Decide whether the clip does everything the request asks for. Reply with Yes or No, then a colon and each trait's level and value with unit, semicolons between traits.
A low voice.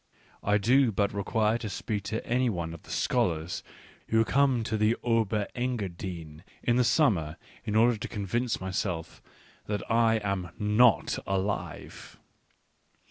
Yes: low, 105 Hz